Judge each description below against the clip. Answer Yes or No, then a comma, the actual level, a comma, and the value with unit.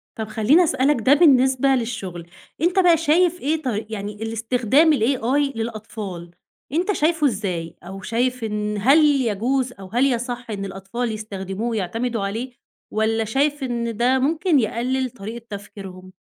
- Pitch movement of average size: Yes, average, 4.5 semitones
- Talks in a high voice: Yes, high, 235 Hz